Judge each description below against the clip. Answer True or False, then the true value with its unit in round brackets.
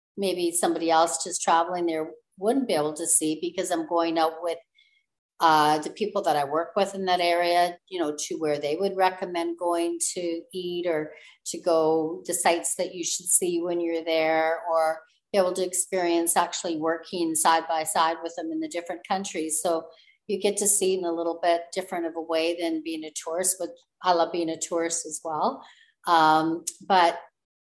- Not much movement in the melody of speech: True (1.9 semitones)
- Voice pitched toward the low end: False (170 Hz)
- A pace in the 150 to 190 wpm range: False (200 wpm)